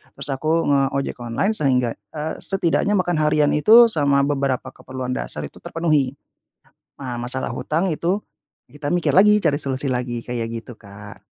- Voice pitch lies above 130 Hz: Yes, medium, 140 Hz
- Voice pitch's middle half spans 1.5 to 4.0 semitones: No, average, 4.4 semitones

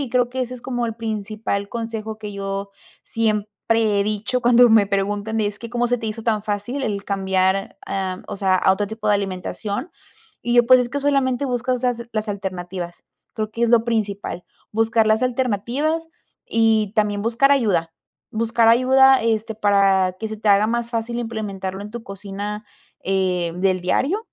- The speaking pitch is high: Yes, high, 220 Hz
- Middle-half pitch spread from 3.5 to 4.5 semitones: No, average, 3.0 semitones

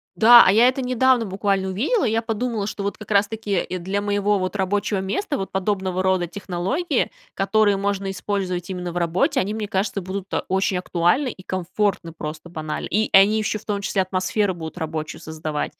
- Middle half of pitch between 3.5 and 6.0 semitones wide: No, narrow, 2.6 semitones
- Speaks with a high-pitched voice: Yes, high, 195 Hz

